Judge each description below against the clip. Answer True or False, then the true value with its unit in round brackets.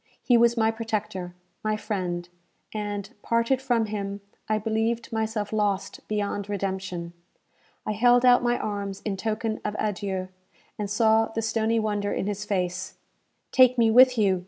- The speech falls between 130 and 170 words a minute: True (155 wpm)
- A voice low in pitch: False (215 Hz)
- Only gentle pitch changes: True (2.1 semitones)